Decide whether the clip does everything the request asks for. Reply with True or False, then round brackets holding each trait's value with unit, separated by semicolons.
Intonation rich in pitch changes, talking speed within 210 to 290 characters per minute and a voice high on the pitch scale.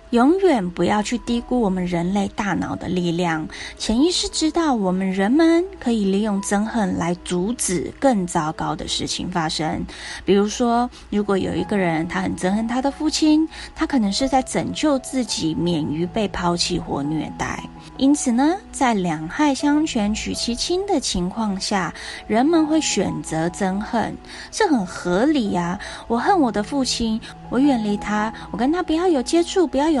True (7.1 semitones; 250 characters per minute; 230 Hz)